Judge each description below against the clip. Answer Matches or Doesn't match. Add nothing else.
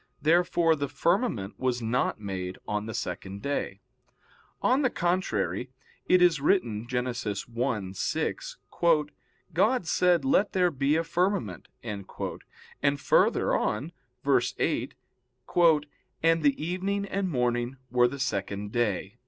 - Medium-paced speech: Doesn't match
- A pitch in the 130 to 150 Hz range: Matches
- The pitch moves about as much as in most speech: Doesn't match